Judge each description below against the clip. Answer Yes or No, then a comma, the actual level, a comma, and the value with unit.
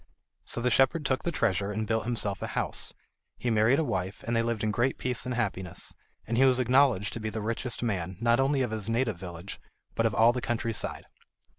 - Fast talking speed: Yes, fast, 230 wpm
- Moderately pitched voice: No, low, 115 Hz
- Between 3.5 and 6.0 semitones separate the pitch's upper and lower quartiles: No, average, 3.1 semitones